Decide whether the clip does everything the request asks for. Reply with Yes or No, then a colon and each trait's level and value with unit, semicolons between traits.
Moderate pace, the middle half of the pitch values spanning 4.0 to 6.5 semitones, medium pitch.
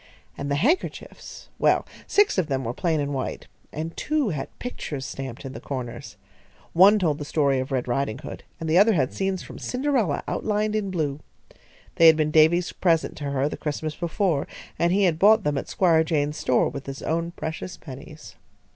Yes: average, 190 wpm; average, 4.9 semitones; medium, 160 Hz